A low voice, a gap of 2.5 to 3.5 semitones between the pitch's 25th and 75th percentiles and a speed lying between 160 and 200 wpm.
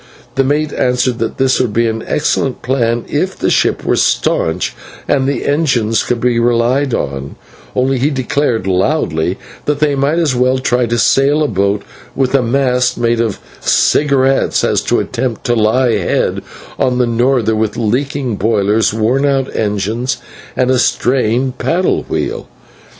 Yes: low, 125 Hz; average, 3.2 semitones; average, 165 wpm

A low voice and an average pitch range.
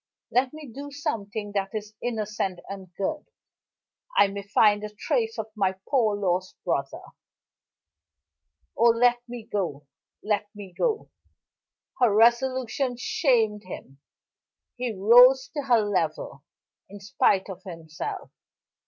No: high, 210 Hz; average, 4.0 semitones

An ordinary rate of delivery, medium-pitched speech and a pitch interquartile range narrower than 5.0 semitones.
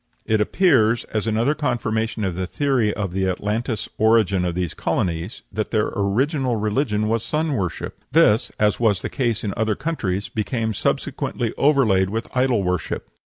No: average, 160 wpm; low, 110 Hz; average, 3.5 semitones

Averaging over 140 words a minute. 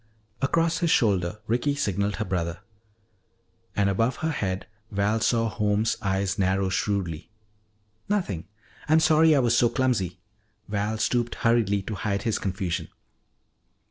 No: slow, 135 wpm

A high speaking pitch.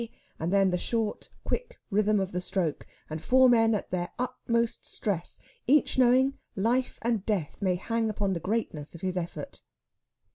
Yes: high, 210 Hz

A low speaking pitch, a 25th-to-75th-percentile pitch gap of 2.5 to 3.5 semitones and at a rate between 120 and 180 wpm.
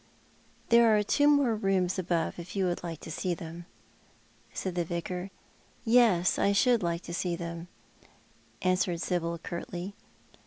No: medium, 180 Hz; average, 2.8 semitones; average, 160 wpm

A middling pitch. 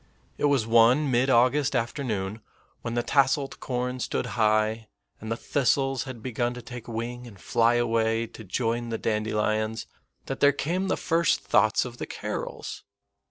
No: low, 120 Hz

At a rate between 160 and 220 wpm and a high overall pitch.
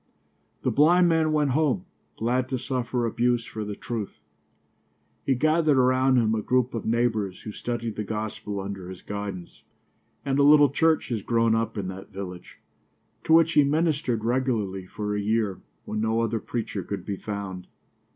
No: average, 170 wpm; low, 115 Hz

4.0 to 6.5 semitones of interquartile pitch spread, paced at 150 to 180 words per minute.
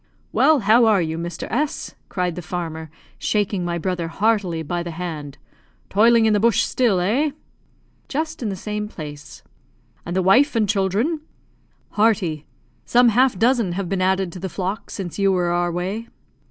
Yes: average, 4.3 semitones; average, 175 wpm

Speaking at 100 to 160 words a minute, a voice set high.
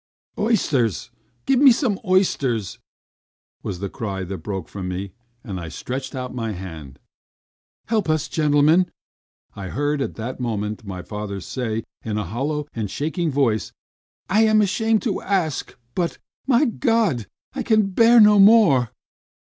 No: average, 145 wpm; low, 135 Hz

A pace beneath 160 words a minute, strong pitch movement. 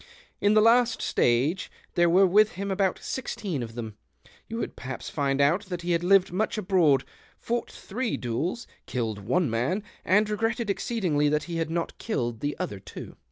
No: average, 190 wpm; wide, 7.2 semitones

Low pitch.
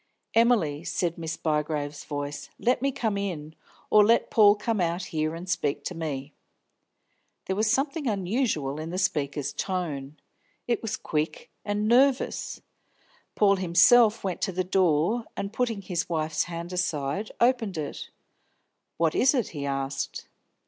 No: medium, 180 Hz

